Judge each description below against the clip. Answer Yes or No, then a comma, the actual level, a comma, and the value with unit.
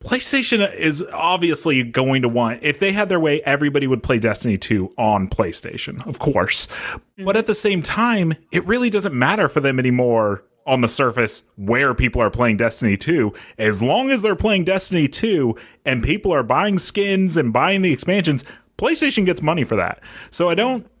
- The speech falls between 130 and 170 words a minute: No, average, 185 wpm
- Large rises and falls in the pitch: Yes, wide, 8.5 semitones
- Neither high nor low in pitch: Yes, medium, 155 Hz